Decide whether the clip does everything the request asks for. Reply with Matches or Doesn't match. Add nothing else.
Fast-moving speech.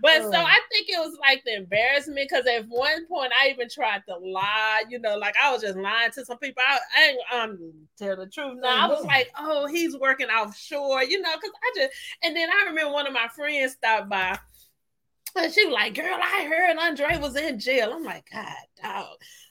Matches